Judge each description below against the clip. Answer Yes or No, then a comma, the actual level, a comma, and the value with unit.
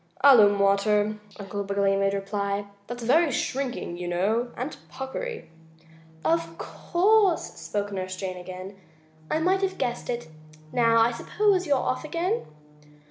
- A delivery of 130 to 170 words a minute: Yes, slow, 135 wpm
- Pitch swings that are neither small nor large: No, wide, 6.3 semitones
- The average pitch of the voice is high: Yes, high, 215 Hz